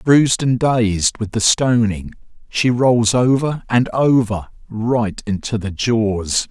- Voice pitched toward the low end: Yes, low, 115 Hz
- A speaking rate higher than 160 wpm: No, average, 140 wpm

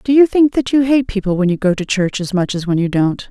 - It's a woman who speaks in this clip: Yes, female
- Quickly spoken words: Yes, fast, 325 wpm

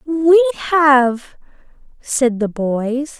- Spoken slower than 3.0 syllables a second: Yes, 2.4 syllables/s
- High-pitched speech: Yes, very high, 280 Hz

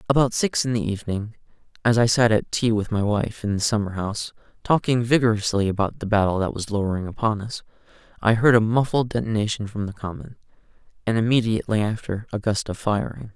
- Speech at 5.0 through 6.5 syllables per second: Yes, 6.0 syllables/s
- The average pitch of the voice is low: Yes, low, 110 Hz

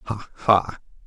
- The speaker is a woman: No, male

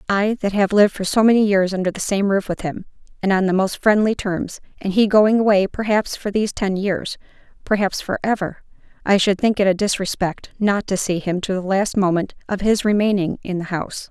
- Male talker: No, female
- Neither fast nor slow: No, fast, 220 wpm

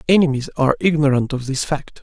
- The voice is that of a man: Yes, male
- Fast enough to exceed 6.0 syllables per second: Yes, 6.2 syllables/s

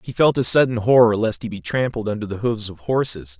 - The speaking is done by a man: Yes, male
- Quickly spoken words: Yes, fast, 250 wpm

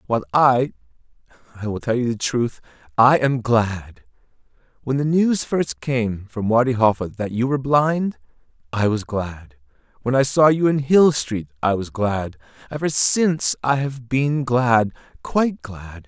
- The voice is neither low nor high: No, low, 120 Hz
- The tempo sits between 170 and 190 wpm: No, average, 155 wpm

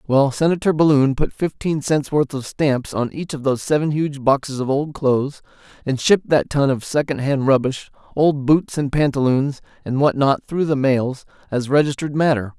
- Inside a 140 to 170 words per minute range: No, average, 185 wpm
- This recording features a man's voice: Yes, male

